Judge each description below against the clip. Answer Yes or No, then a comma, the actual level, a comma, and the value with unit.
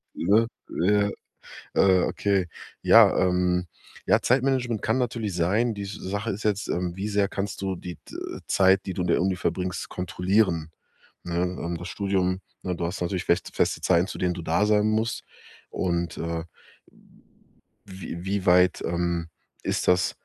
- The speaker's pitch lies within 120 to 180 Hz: No, very low, 95 Hz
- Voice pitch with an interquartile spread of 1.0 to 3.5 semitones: Yes, narrow, 2.5 semitones